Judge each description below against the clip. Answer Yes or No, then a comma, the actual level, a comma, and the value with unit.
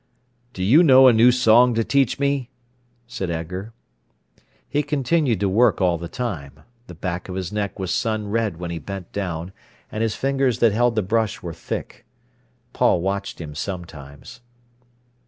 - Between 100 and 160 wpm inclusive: No, average, 170 wpm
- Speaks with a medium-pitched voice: No, low, 105 Hz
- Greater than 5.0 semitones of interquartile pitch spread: Yes, wide, 5.5 semitones